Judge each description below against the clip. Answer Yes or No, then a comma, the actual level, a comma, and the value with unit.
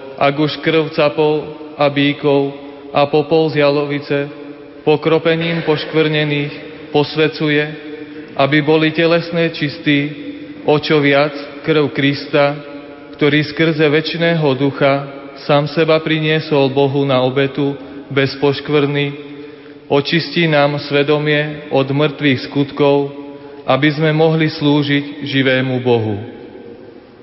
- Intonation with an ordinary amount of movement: No, narrow, 1.3 semitones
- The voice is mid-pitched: Yes, medium, 145 Hz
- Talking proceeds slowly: Yes, slow, 100 wpm